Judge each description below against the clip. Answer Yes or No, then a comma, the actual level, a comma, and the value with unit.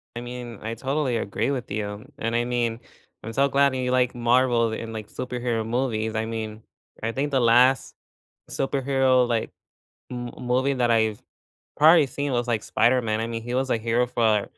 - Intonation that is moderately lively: No, narrow, 2.3 semitones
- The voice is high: No, low, 120 Hz